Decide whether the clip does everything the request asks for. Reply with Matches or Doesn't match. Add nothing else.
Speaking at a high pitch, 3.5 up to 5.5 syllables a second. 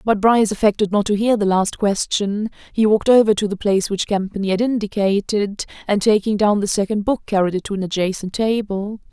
Doesn't match